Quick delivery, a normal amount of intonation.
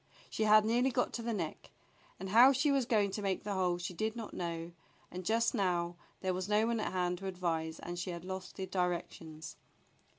Yes: fast, 220 wpm; average, 3.8 semitones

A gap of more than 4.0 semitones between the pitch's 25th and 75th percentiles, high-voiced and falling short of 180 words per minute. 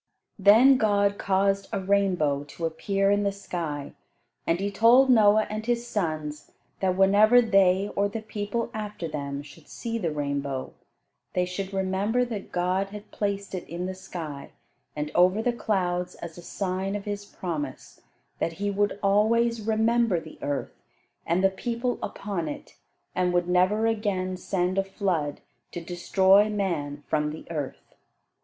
No: average, 3.2 semitones; high, 195 Hz; average, 160 wpm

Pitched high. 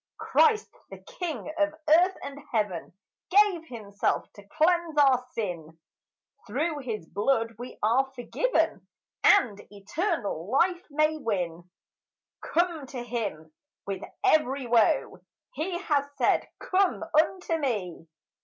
Yes: very high, 270 Hz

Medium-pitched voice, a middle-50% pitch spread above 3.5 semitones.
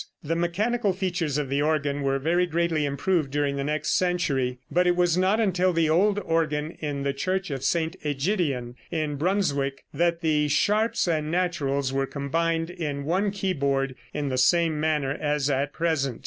Yes: medium, 155 Hz; average, 4.0 semitones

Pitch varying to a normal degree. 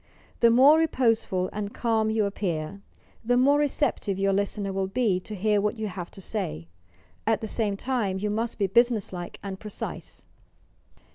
Yes: average, 3.2 semitones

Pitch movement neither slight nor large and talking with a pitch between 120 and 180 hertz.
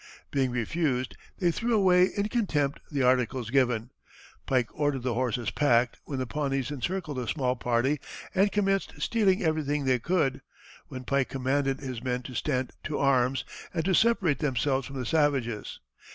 Yes: average, 4.0 semitones; low, 135 Hz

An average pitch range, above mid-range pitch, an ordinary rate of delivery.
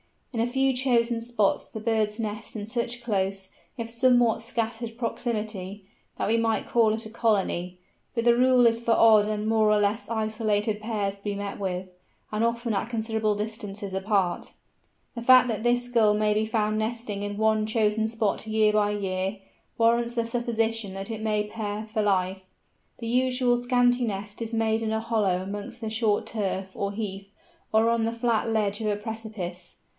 No: narrow, 2.0 semitones; high, 220 Hz; average, 185 wpm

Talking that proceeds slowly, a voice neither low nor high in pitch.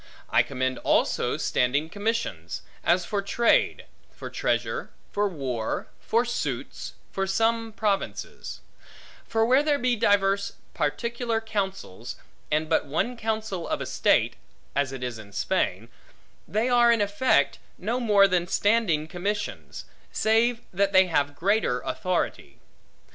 No: slow, 130 wpm; high, 200 Hz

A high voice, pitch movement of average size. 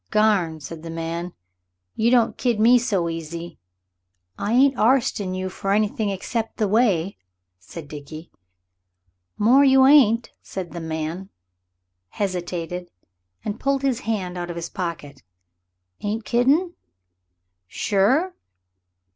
No: high, 200 Hz; wide, 5.7 semitones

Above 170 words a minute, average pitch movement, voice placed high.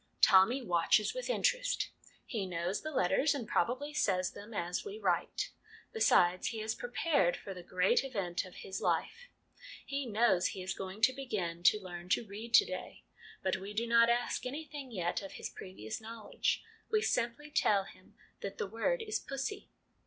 No: average, 180 wpm; wide, 6.6 semitones; high, 220 Hz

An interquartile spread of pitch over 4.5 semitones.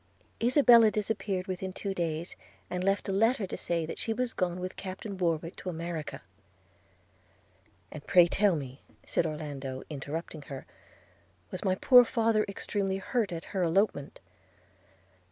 No: average, 4.0 semitones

